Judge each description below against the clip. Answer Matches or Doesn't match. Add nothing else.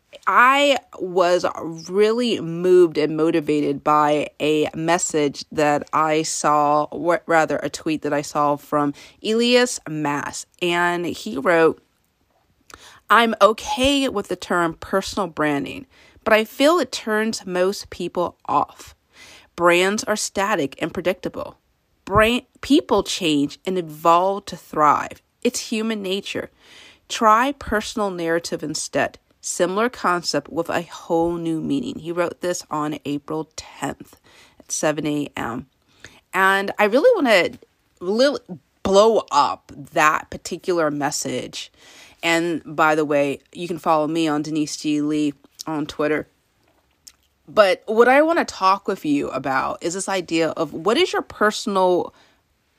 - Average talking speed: Doesn't match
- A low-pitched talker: Doesn't match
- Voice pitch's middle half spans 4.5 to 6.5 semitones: Matches